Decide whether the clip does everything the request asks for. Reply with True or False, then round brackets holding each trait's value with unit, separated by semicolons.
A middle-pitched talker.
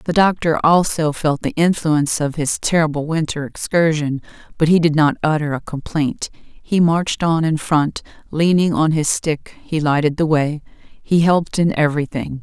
True (155 Hz)